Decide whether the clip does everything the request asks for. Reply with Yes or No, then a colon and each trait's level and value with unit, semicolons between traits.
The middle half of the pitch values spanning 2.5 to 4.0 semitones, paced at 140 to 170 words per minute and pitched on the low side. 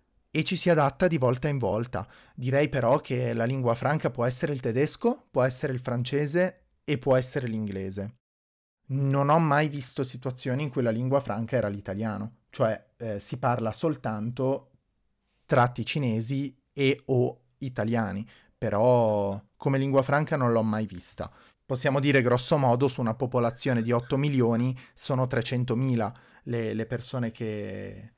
Yes: average, 3.5 semitones; average, 155 wpm; low, 125 Hz